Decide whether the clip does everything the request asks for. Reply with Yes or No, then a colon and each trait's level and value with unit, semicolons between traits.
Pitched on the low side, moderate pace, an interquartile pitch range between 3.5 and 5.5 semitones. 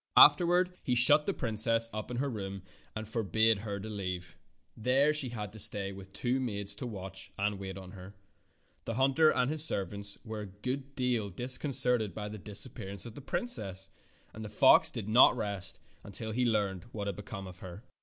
Yes: low, 110 Hz; average, 195 wpm; average, 4.2 semitones